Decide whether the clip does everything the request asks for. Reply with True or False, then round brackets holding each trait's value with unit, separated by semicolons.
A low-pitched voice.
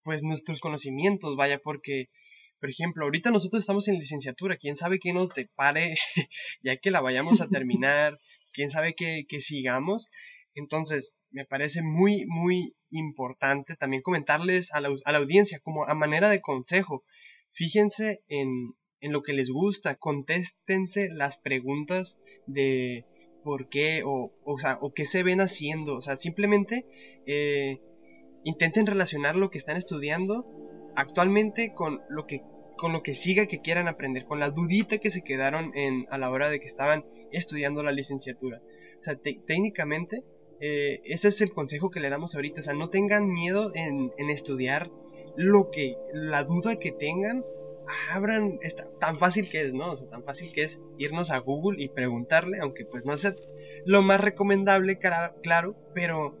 False (155 Hz)